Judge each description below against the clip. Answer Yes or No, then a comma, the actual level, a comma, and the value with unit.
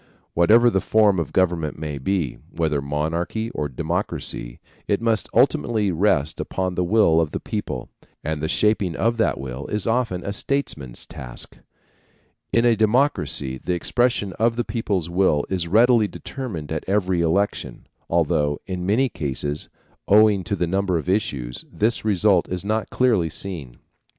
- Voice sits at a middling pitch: No, very low, 95 Hz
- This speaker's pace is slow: No, average, 155 wpm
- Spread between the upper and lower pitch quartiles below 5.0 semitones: No, wide, 5.6 semitones